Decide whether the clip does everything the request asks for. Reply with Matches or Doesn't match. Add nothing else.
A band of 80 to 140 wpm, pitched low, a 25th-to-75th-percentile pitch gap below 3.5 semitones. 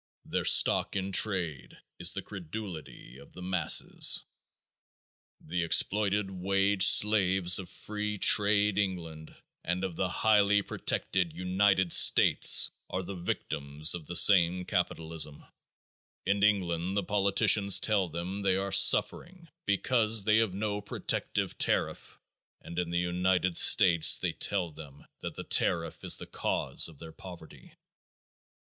Matches